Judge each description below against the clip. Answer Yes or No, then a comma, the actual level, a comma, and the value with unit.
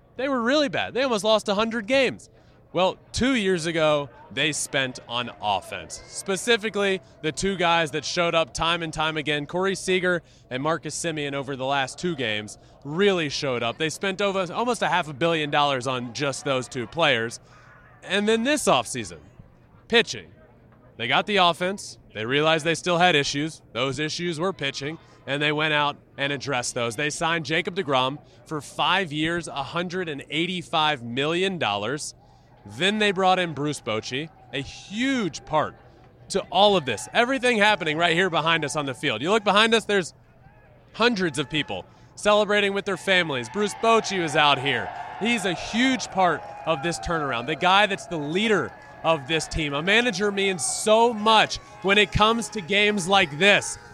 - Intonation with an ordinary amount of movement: No, wide, 5.9 semitones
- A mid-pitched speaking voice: Yes, medium, 165 Hz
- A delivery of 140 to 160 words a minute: No, average, 175 wpm